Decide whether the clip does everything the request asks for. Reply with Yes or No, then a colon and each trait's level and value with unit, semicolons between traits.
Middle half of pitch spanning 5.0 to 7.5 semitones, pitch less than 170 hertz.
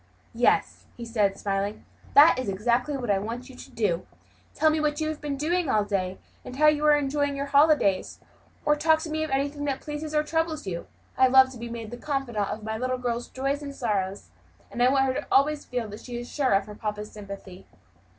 No: wide, 5.5 semitones; very high, 255 Hz